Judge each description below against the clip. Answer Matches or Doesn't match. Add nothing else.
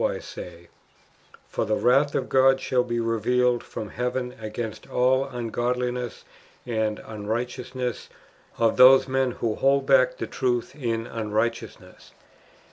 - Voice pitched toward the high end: Doesn't match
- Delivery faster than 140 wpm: Doesn't match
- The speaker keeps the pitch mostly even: Matches